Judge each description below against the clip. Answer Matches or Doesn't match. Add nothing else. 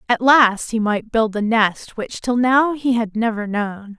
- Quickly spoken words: Matches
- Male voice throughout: Doesn't match